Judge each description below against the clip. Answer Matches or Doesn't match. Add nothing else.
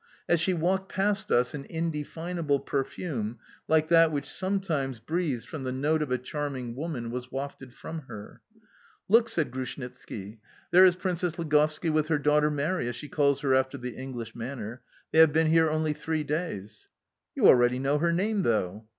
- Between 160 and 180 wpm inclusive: Matches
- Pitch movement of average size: Matches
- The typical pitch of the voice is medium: Matches